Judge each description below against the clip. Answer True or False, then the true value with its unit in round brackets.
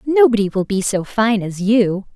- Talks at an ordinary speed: True (195 wpm)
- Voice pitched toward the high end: True (215 Hz)